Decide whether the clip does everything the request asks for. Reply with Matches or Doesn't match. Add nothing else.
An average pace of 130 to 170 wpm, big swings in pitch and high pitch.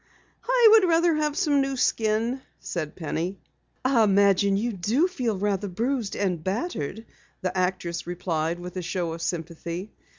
Matches